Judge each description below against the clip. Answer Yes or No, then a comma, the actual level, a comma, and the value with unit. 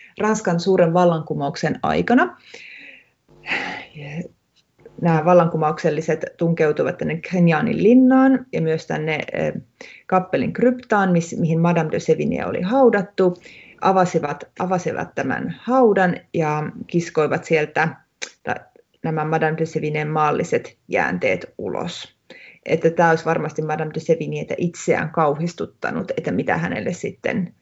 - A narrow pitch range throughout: No, average, 3.0 semitones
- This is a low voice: No, medium, 165 Hz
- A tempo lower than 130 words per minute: Yes, average, 105 wpm